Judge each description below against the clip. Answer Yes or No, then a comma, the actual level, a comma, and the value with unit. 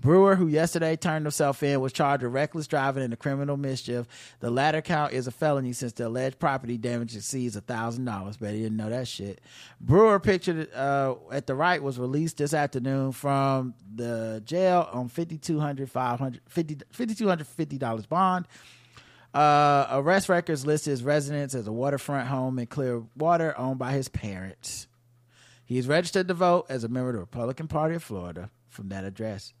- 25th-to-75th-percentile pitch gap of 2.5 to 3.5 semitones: No, average, 4.2 semitones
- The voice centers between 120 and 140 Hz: Yes, low, 135 Hz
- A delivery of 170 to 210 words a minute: Yes, average, 175 wpm